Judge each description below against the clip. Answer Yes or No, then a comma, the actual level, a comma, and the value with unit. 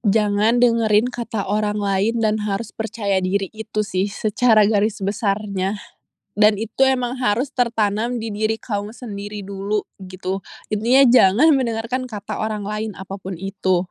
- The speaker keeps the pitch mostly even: Yes, narrow, 2.2 semitones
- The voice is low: No, high, 210 Hz